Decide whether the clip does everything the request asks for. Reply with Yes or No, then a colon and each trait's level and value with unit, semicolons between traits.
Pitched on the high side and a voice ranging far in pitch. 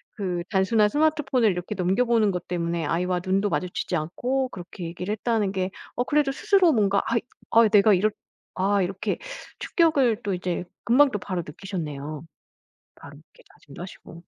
No: high, 195 Hz; average, 4.6 semitones